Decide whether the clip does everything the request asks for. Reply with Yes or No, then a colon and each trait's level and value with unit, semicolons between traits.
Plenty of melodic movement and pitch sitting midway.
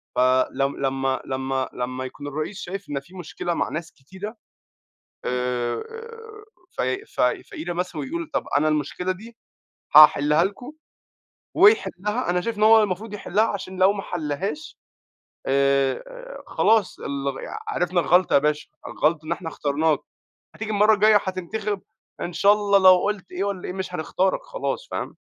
Yes: wide, 6.2 semitones; medium, 180 Hz